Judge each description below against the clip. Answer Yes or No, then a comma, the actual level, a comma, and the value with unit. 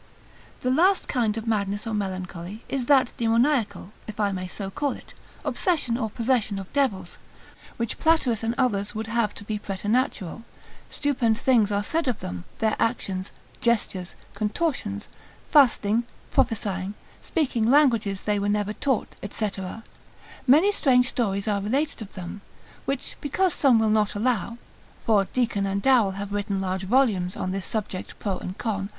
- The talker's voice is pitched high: Yes, high, 220 Hz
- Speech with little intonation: No, average, 4.1 semitones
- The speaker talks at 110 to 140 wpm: No, average, 155 wpm